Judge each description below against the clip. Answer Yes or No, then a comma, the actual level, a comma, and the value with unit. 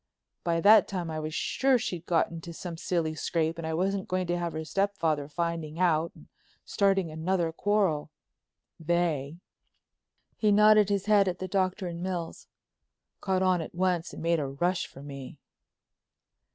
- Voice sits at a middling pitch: Yes, medium, 175 Hz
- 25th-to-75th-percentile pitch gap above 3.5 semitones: No, average, 2.7 semitones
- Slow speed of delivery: No, average, 165 wpm